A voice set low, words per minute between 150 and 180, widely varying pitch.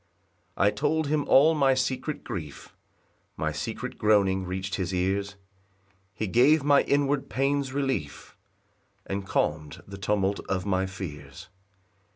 No: low, 100 Hz; slow, 135 wpm; wide, 6.6 semitones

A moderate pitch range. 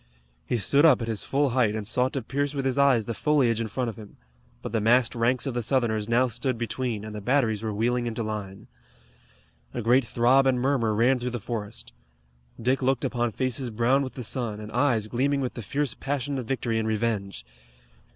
Yes: average, 3.0 semitones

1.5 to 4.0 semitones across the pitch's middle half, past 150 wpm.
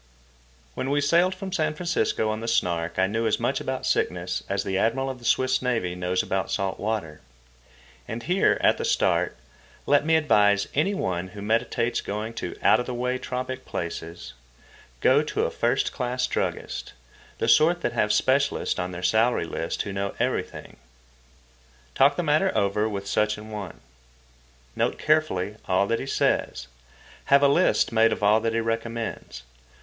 No: average, 5.3 semitones; average, 175 wpm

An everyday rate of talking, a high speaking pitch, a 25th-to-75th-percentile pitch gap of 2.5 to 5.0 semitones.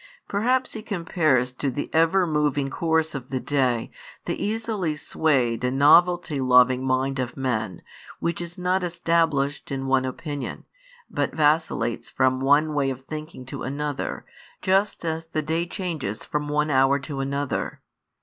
No: average, 150 wpm; medium, 145 Hz; average, 3.9 semitones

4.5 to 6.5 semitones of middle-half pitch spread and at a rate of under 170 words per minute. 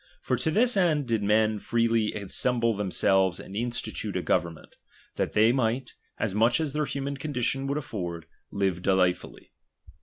Yes: wide, 5.4 semitones; average, 155 wpm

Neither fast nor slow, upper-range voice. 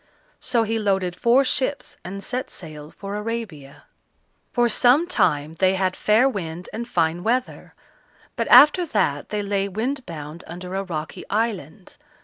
Yes: average, 150 wpm; high, 200 Hz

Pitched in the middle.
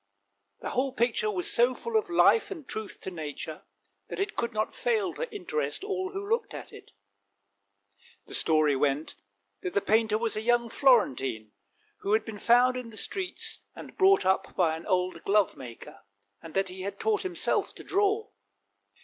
No: high, 230 Hz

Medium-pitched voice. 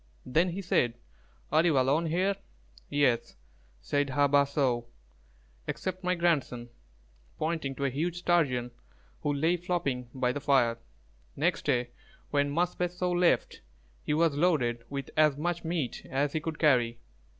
Yes: medium, 145 Hz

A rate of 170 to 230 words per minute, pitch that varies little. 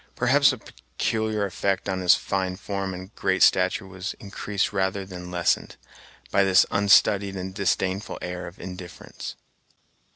No: average, 140 wpm; narrow, 1.4 semitones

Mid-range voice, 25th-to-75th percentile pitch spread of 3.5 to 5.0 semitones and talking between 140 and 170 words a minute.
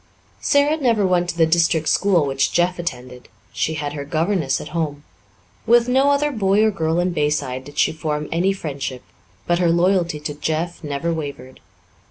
No: medium, 165 Hz; average, 4.1 semitones; average, 180 wpm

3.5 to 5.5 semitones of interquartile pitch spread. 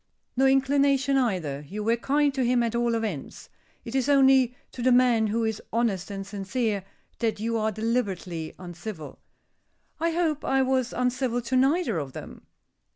Yes: average, 4.1 semitones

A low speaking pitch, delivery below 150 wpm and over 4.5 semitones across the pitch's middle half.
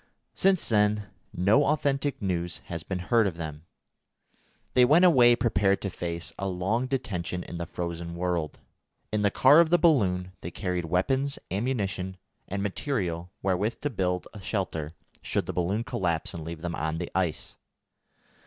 No: very low, 95 Hz; average, 165 wpm; wide, 5.4 semitones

